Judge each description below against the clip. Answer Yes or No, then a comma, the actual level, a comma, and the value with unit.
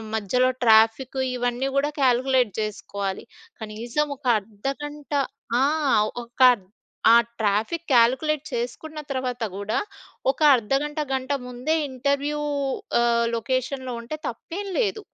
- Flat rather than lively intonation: No, average, 3.3 semitones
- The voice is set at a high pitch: Yes, very high, 255 Hz